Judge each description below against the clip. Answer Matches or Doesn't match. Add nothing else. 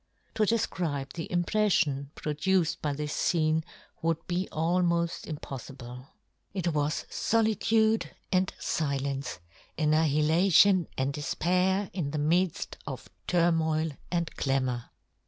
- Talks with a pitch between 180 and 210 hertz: Doesn't match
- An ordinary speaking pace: Doesn't match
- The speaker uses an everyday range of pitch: Matches